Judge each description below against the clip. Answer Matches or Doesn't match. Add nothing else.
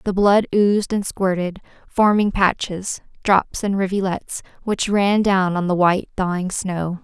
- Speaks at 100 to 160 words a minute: Matches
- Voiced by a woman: Matches